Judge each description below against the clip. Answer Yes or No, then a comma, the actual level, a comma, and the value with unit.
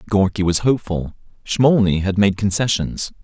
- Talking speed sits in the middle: No, slow, 130 wpm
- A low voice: Yes, low, 100 Hz